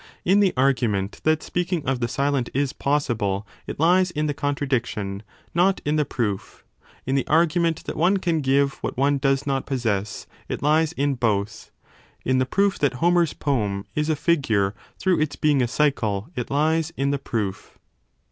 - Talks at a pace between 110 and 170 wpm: No, average, 185 wpm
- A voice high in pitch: No, medium, 140 Hz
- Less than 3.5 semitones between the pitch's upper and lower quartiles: No, average, 4.6 semitones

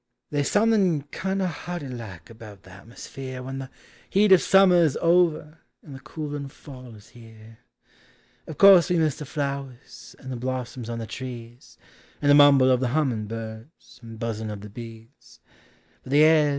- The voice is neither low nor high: No, low, 130 Hz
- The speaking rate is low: No, average, 175 wpm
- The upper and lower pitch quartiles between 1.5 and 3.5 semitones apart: No, average, 5.1 semitones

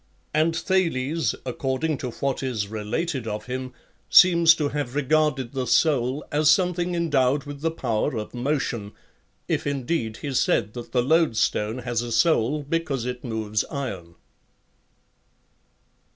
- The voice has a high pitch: No, low, 135 Hz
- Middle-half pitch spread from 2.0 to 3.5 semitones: No, average, 4.5 semitones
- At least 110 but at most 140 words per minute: Yes, slow, 135 wpm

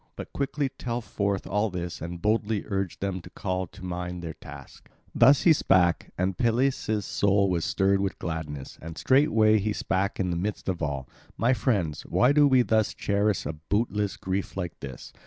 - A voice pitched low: Yes, low, 100 Hz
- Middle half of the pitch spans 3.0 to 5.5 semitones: Yes, average, 3.8 semitones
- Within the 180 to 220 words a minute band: Yes, average, 185 wpm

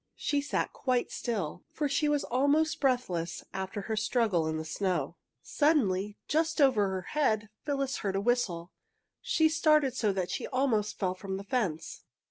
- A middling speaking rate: Yes, average, 165 wpm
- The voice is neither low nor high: No, high, 230 Hz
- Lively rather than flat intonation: Yes, wide, 6.9 semitones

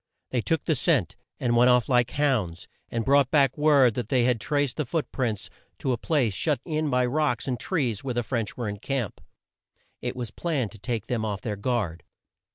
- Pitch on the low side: Yes, low, 125 Hz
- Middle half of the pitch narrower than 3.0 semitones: No, average, 3.8 semitones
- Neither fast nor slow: No, fast, 210 wpm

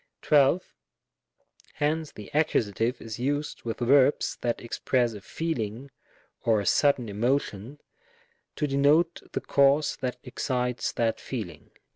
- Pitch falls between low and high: No, low, 125 Hz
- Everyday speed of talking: No, slow, 125 wpm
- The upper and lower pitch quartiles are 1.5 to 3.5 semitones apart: No, average, 4.1 semitones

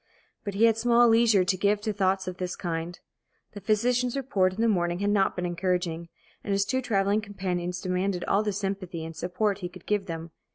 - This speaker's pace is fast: Yes, fast, 210 wpm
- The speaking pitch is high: Yes, high, 195 Hz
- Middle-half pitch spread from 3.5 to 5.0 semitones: No, average, 2.9 semitones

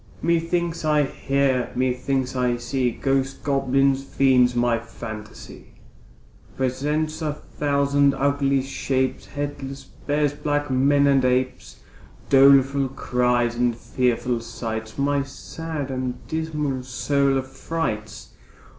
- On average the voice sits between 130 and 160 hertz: Yes, low, 135 Hz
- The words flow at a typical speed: No, slow, 105 wpm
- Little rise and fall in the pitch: Yes, narrow, 2.2 semitones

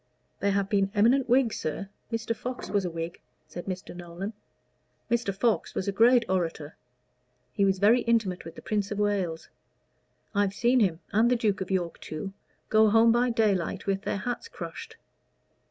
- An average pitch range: Yes, average, 3.5 semitones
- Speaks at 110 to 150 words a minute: No, average, 175 wpm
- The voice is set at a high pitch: Yes, high, 200 Hz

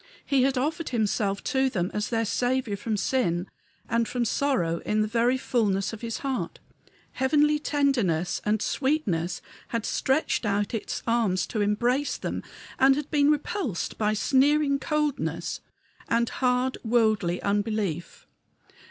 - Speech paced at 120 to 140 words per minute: Yes, slow, 135 wpm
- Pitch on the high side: Yes, high, 235 Hz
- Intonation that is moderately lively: Yes, average, 4.6 semitones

